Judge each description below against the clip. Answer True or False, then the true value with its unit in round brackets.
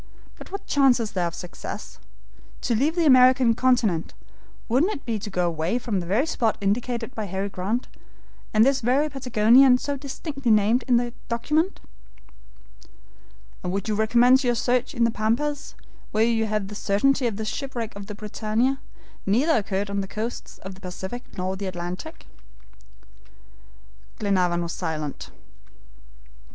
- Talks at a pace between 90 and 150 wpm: False (160 wpm)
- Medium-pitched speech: False (225 Hz)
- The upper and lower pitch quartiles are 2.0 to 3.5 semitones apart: False (4.4 semitones)